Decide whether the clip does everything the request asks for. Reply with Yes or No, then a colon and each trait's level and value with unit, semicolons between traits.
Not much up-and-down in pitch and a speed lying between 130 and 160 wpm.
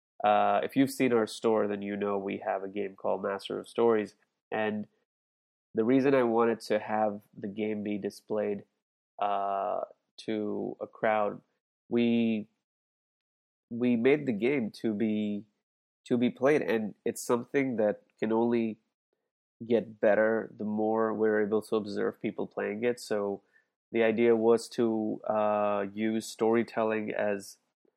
Yes: narrow, 1.9 semitones; average, 145 wpm